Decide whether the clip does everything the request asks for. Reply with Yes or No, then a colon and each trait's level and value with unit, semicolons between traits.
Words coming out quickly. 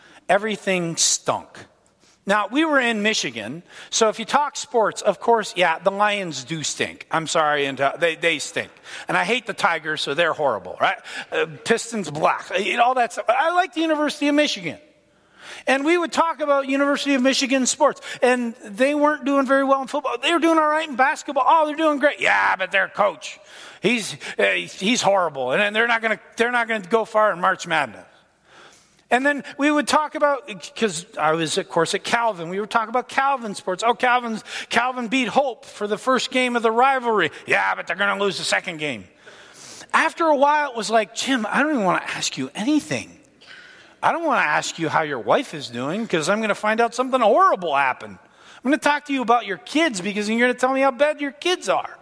Yes: fast, 215 wpm